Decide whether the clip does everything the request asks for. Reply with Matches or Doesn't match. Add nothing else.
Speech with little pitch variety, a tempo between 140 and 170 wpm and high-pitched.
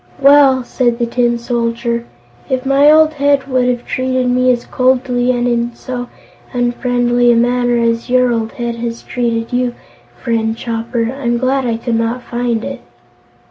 Matches